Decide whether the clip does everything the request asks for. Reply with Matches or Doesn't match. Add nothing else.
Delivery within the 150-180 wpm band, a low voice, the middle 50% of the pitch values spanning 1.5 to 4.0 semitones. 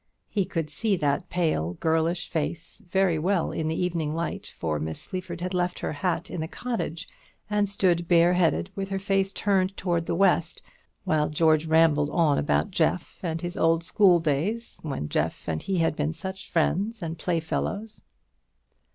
Doesn't match